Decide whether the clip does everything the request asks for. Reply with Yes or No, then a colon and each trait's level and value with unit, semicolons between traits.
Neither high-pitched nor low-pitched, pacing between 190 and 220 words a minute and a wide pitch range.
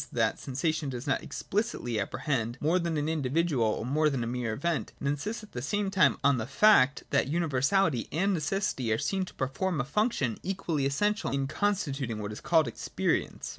Yes: medium, 145 Hz; average, 195 wpm; wide, 6.3 semitones